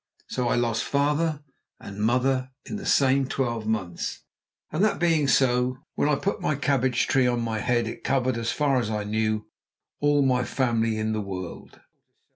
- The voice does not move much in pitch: No, average, 3.8 semitones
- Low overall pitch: Yes, low, 125 Hz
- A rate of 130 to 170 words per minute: No, average, 180 wpm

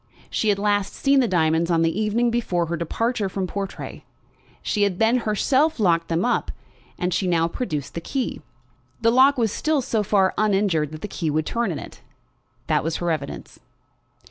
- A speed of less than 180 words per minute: No, average, 185 wpm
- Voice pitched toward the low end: No, high, 200 Hz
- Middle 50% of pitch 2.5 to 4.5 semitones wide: No, wide, 5.6 semitones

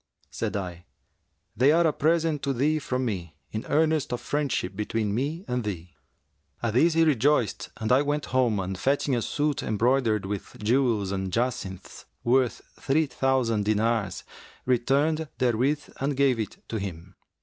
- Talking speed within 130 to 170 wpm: Yes, average, 160 wpm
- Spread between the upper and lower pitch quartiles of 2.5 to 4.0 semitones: No, average, 5.2 semitones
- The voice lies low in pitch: Yes, low, 125 Hz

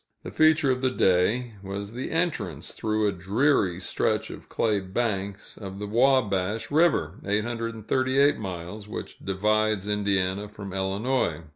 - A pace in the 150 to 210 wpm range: No, slow, 135 wpm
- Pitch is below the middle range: Yes, low, 105 Hz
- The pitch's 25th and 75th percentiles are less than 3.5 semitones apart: No, average, 4.1 semitones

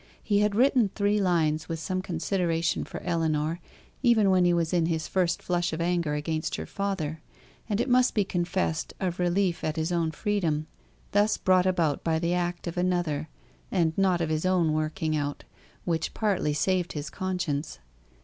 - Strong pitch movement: No, average, 2.9 semitones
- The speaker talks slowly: No, average, 180 wpm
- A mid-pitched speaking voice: Yes, medium, 175 Hz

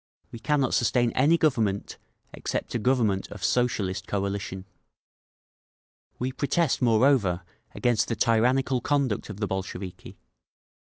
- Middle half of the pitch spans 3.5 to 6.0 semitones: Yes, average, 4.5 semitones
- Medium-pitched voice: No, low, 115 Hz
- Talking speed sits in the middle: No, slow, 115 wpm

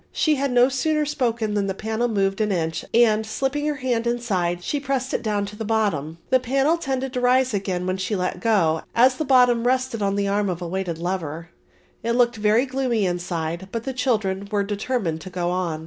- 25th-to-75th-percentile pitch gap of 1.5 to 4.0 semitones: No, average, 5.3 semitones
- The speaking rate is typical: No, fast, 215 wpm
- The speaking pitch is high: Yes, high, 215 Hz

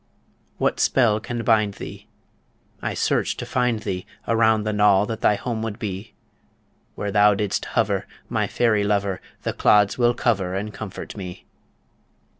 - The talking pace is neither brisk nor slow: Yes, average, 155 wpm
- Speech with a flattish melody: Yes, narrow, 2.0 semitones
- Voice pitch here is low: Yes, low, 105 Hz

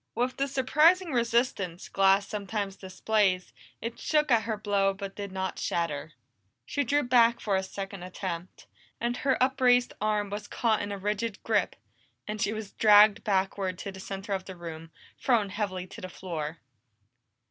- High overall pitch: Yes, high, 205 Hz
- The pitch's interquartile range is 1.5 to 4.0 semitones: Yes, average, 3.6 semitones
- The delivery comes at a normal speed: Yes, average, 170 wpm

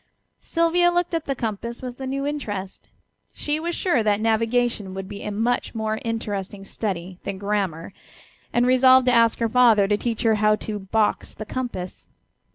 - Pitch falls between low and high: No, high, 225 Hz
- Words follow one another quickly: No, average, 175 wpm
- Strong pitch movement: No, average, 3.8 semitones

